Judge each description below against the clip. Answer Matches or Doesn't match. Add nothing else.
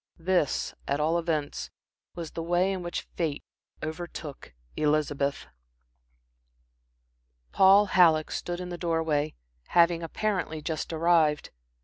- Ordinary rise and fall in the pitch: Doesn't match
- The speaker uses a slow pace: Matches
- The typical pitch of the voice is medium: Matches